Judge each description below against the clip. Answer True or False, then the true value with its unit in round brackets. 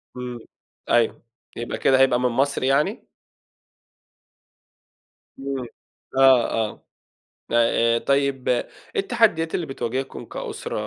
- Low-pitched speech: True (130 Hz)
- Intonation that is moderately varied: False (2.1 semitones)